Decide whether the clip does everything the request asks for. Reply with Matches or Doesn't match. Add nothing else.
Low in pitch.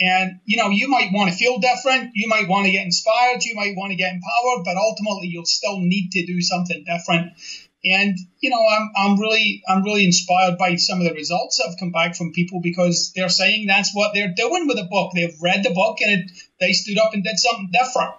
Doesn't match